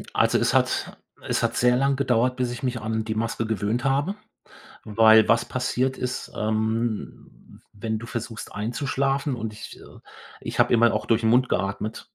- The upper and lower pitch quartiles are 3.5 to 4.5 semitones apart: No, narrow, 2.4 semitones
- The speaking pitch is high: No, low, 115 Hz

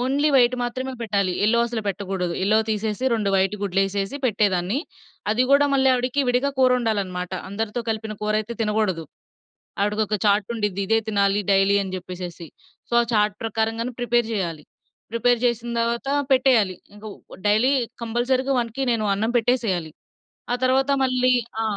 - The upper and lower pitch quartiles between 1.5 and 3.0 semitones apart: No, average, 3.5 semitones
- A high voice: Yes, high, 220 Hz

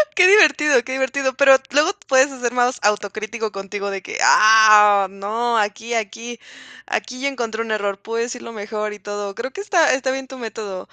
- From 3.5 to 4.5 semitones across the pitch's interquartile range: Yes, average, 4.0 semitones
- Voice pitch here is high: Yes, high, 230 Hz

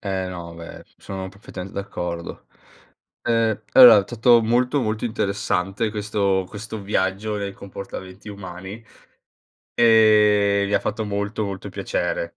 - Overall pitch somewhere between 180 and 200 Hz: No, low, 100 Hz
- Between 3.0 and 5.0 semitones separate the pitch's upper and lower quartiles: No, narrow, 2.4 semitones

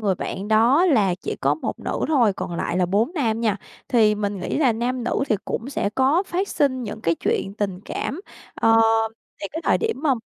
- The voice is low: No, high, 225 Hz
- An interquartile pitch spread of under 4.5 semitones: No, average, 5.2 semitones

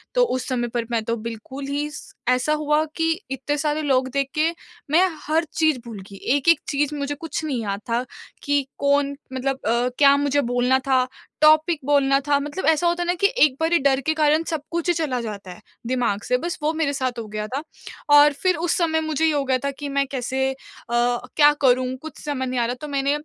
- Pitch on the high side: Yes, very high, 280 Hz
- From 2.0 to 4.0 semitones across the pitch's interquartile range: Yes, average, 3.3 semitones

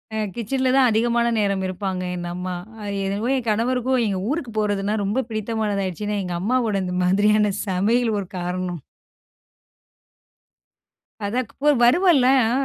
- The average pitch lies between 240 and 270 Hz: No, high, 210 Hz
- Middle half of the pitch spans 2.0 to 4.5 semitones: Yes, average, 3.8 semitones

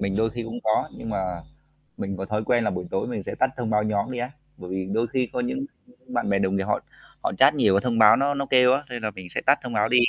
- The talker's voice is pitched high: No, low, 110 Hz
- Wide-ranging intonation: No, average, 4.1 semitones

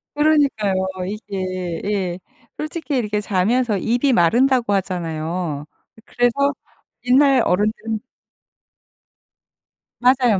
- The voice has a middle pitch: No, high, 220 Hz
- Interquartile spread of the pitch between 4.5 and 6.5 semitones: Yes, average, 5.3 semitones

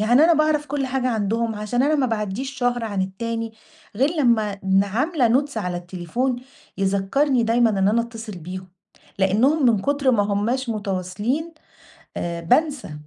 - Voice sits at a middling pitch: No, high, 230 Hz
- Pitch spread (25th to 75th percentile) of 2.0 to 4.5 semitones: No, average, 5.1 semitones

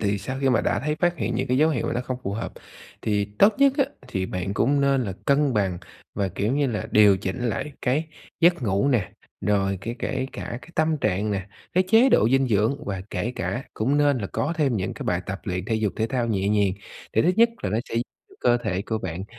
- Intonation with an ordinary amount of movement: No, wide, 5.8 semitones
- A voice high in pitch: No, low, 115 Hz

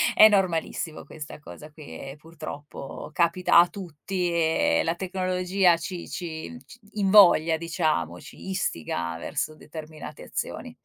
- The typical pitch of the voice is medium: Yes, medium, 165 Hz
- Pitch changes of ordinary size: Yes, average, 3.1 semitones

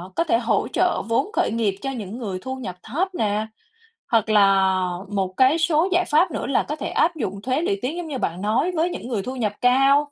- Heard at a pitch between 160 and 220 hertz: No, very high, 255 Hz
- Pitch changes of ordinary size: No, wide, 6.9 semitones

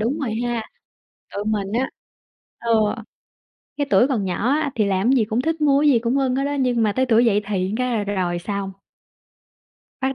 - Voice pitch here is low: No, high, 235 Hz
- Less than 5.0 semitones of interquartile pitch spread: Yes, average, 4.5 semitones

